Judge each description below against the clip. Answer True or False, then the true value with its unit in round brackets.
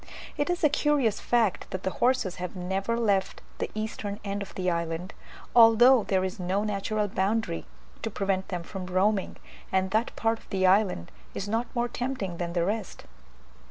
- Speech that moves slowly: False (180 wpm)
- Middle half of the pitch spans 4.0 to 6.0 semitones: False (3.4 semitones)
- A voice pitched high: True (200 Hz)